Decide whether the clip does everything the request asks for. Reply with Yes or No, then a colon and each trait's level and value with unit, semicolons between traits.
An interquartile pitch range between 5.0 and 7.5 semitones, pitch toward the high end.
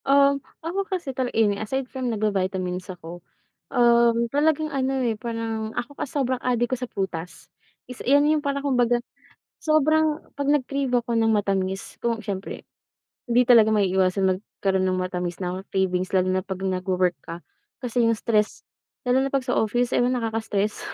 Yes: wide, 5.5 semitones; high, 230 Hz